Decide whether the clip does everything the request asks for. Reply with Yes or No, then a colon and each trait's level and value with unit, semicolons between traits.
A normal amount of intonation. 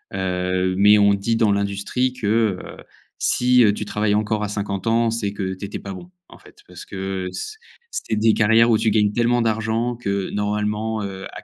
No: narrow, 2.3 semitones